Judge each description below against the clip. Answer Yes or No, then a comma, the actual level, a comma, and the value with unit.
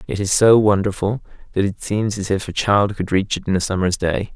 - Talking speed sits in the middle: No, fast, 250 wpm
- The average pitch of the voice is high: No, low, 100 Hz